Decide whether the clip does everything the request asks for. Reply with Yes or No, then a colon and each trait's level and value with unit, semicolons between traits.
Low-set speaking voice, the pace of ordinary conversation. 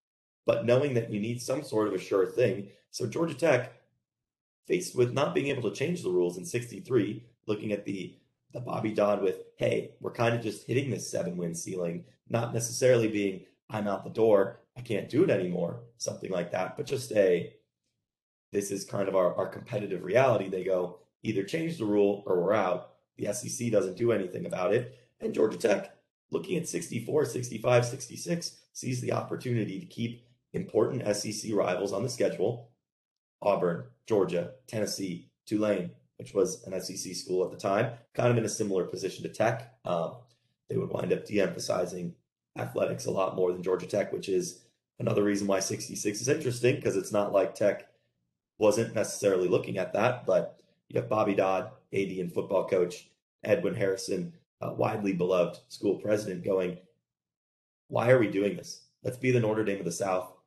Yes: low, 105 Hz; average, 185 wpm